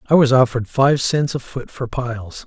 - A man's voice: Yes, male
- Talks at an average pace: No, fast, 220 wpm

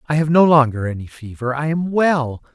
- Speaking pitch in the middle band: Yes, medium, 145 Hz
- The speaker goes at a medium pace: No, fast, 210 wpm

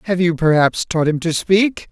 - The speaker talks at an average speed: No, fast, 220 wpm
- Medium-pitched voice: Yes, medium, 170 Hz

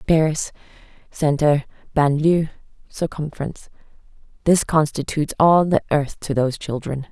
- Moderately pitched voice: Yes, medium, 150 Hz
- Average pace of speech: No, slow, 100 wpm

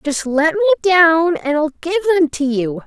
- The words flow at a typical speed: No, fast, 210 wpm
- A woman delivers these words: Yes, female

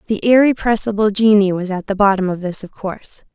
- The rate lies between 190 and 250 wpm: Yes, average, 200 wpm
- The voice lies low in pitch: No, high, 200 Hz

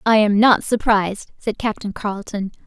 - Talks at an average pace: Yes, average, 160 wpm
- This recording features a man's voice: No, female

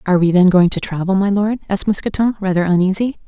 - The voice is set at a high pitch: Yes, high, 195 Hz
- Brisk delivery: Yes, fast, 220 wpm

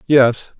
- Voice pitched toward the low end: Yes, low, 130 Hz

